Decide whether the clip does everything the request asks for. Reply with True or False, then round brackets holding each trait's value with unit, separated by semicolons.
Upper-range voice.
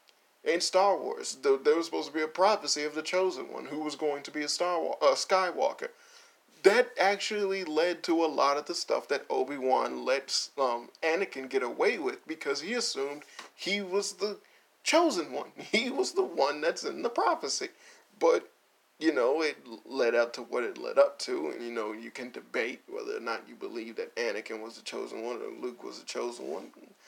True (290 Hz)